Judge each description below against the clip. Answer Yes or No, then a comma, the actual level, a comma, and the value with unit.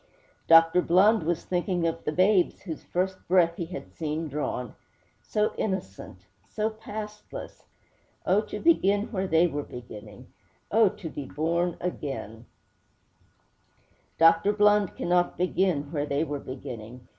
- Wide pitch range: No, average, 4.8 semitones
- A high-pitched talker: No, medium, 170 Hz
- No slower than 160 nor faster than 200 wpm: No, slow, 135 wpm